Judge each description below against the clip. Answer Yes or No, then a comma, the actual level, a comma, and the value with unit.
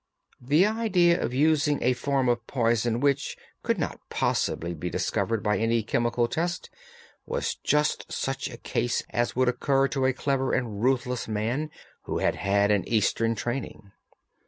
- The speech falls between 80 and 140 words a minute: No, average, 160 wpm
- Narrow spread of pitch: No, average, 3.6 semitones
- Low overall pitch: Yes, low, 125 Hz